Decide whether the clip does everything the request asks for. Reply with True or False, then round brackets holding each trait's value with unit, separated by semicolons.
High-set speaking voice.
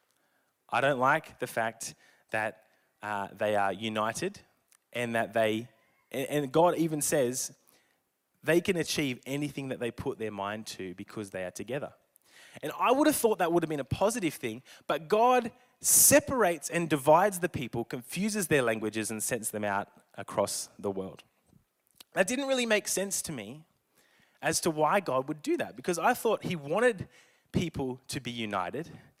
False (140 Hz)